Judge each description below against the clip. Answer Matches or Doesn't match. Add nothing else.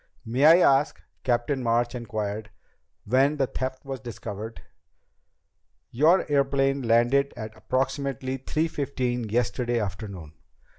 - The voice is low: Matches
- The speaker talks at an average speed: Doesn't match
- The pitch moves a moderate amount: Matches